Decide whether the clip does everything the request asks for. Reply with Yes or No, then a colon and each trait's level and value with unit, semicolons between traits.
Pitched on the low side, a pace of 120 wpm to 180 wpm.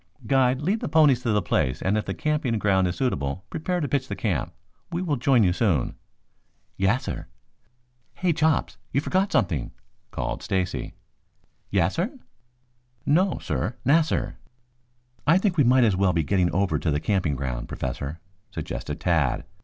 Yes: low, 110 Hz; average, 160 wpm